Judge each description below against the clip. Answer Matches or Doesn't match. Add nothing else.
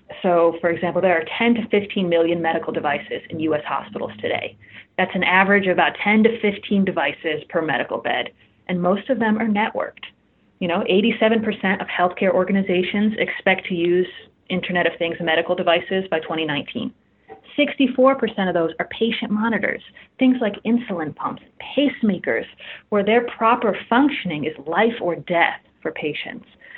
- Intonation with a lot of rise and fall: Doesn't match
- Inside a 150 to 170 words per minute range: Matches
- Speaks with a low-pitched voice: Doesn't match